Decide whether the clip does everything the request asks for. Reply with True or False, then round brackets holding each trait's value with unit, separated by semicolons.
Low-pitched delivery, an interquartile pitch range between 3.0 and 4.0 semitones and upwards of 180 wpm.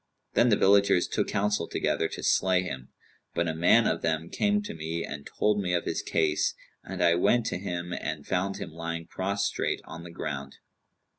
True (85 Hz; 3.4 semitones; 200 wpm)